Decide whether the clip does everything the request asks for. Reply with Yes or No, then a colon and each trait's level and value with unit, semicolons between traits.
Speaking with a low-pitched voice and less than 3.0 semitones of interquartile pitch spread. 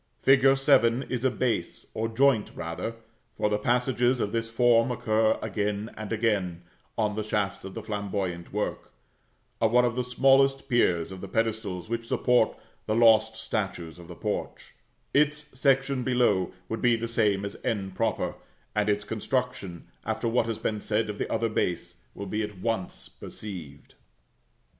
No: low, 110 Hz; average, 3.3 semitones